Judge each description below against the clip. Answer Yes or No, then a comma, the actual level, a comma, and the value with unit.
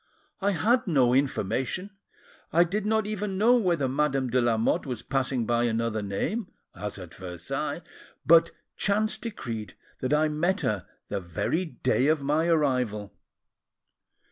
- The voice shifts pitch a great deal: Yes, wide, 7.9 semitones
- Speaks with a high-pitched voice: No, medium, 140 Hz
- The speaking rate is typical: Yes, average, 145 wpm